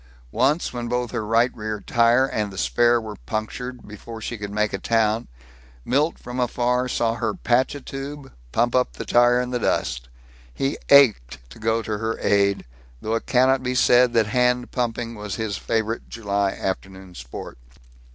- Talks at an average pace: Yes, average, 180 wpm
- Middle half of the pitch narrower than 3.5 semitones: Yes, average, 2.7 semitones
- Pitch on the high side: No, low, 115 Hz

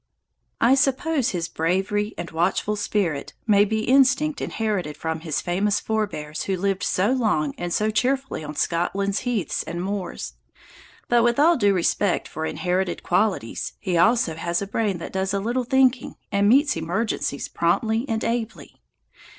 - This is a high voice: Yes, high, 200 Hz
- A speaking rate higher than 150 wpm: Yes, average, 160 wpm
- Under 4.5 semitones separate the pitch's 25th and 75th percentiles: No, average, 5.0 semitones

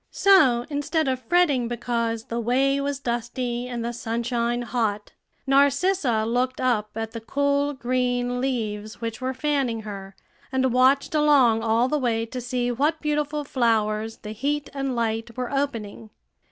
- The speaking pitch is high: Yes, high, 245 Hz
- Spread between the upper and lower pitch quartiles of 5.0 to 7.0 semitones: No, average, 3.3 semitones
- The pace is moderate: Yes, average, 155 wpm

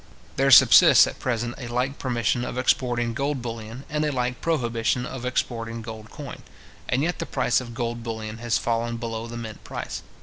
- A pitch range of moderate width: No, narrow, 1.8 semitones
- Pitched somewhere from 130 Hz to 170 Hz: No, low, 120 Hz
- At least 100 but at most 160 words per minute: No, average, 190 wpm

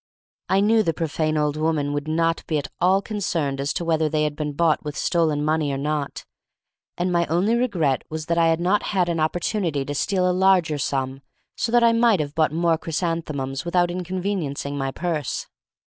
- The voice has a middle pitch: Yes, medium, 165 Hz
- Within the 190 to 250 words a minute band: Yes, average, 200 wpm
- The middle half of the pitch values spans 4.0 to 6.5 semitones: No, average, 3.4 semitones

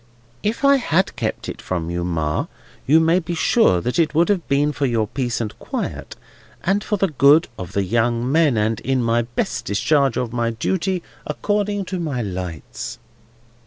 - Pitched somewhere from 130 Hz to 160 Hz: Yes, low, 135 Hz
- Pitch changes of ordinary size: No, wide, 7.3 semitones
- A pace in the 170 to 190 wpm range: Yes, average, 180 wpm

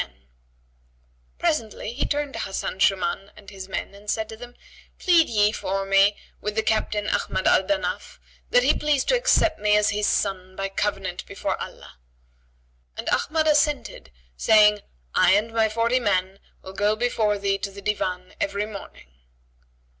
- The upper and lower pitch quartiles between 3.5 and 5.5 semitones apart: No, average, 3.0 semitones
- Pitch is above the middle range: Yes, high, 210 Hz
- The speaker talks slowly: No, average, 165 wpm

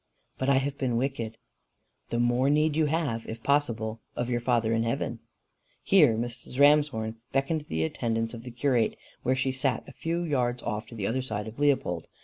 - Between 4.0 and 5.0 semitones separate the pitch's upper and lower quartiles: No, average, 3.6 semitones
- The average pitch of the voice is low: Yes, low, 125 Hz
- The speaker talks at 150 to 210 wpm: Yes, average, 190 wpm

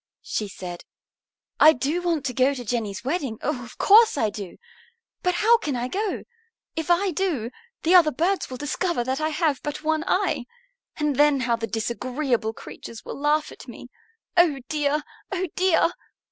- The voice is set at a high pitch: Yes, very high, 295 Hz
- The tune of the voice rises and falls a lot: Yes, wide, 5.8 semitones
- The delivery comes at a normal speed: Yes, average, 175 wpm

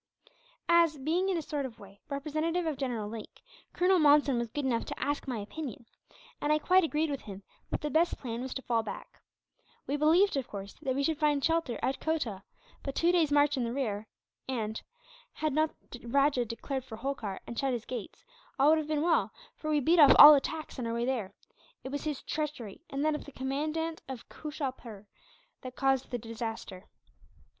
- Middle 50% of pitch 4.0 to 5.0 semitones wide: Yes, average, 4.5 semitones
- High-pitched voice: Yes, very high, 275 Hz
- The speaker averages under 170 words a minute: No, fast, 205 wpm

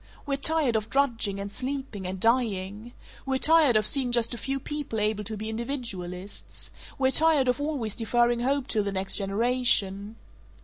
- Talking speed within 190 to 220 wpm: No, average, 170 wpm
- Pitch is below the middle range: No, high, 235 Hz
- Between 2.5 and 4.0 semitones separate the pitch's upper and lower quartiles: No, average, 4.6 semitones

